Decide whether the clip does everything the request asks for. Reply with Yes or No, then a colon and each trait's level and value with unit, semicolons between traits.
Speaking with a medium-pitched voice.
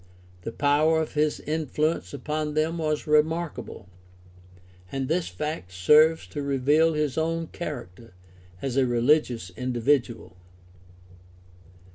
Yes: medium, 150 Hz